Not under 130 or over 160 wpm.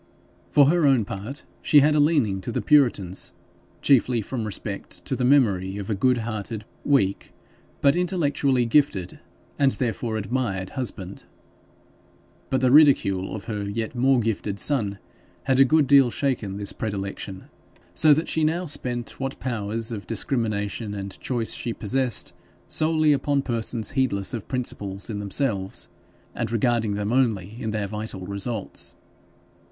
Yes: average, 150 wpm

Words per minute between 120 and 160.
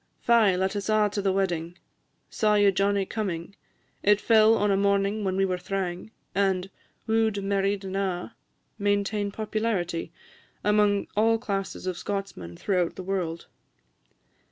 Yes: average, 150 wpm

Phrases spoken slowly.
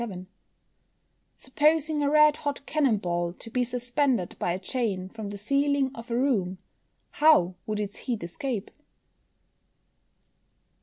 Yes: slow, 130 wpm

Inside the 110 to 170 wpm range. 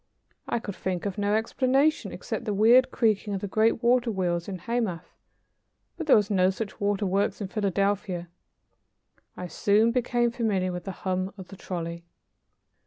Yes: average, 165 wpm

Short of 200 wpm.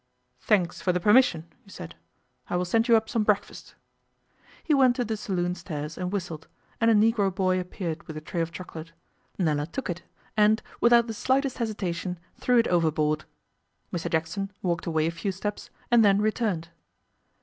Yes: average, 180 wpm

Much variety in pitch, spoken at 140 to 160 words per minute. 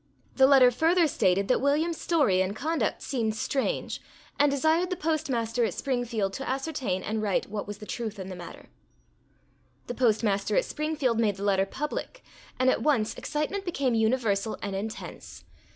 No: wide, 6.1 semitones; average, 170 wpm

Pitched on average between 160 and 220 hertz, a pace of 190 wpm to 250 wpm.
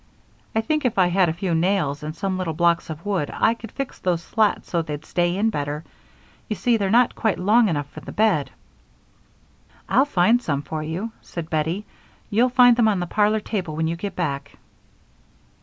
Yes: medium, 185 Hz; average, 200 wpm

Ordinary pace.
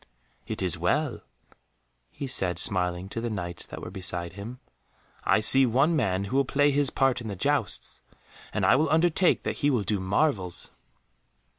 Yes: average, 175 wpm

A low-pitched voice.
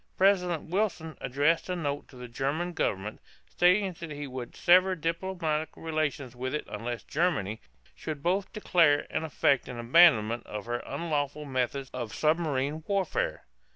No: medium, 150 Hz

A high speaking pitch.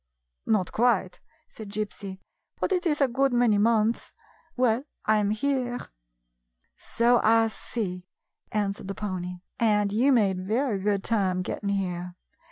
Yes: high, 215 Hz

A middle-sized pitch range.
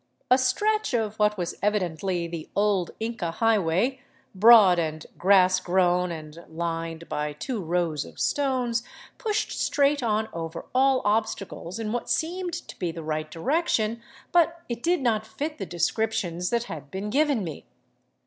No: wide, 6.4 semitones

